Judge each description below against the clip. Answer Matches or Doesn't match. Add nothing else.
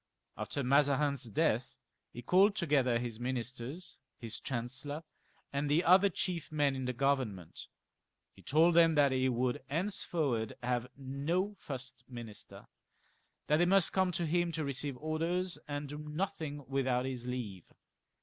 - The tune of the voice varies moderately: Matches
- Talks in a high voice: Doesn't match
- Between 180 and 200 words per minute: Doesn't match